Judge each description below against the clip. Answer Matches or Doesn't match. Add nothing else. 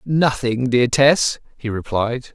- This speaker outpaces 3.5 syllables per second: Doesn't match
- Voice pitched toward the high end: Doesn't match